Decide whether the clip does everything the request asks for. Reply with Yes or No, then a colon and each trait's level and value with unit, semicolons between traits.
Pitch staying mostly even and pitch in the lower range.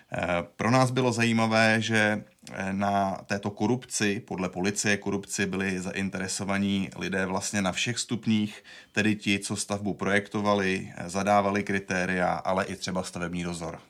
Yes: narrow, 1.8 semitones; low, 100 Hz